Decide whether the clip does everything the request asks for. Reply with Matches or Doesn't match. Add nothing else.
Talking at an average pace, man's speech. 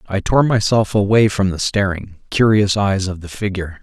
Matches